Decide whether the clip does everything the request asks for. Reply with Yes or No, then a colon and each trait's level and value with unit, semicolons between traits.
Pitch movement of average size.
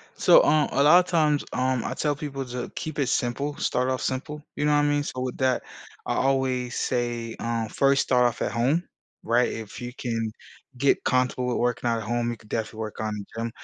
Yes: average, 3.0 semitones